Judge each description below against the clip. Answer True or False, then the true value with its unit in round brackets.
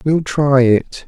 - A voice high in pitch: False (135 Hz)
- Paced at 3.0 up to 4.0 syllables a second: True (3.1 syllables/s)